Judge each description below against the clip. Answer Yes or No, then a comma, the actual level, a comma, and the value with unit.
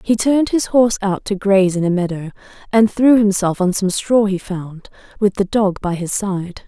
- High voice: Yes, high, 200 Hz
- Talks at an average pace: No, fast, 215 wpm